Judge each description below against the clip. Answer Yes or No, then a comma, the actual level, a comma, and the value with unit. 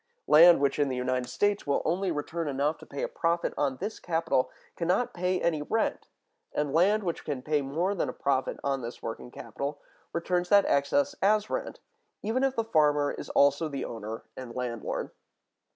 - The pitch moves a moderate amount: Yes, average, 4.9 semitones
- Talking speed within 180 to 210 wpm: Yes, average, 190 wpm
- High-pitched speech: No, medium, 155 Hz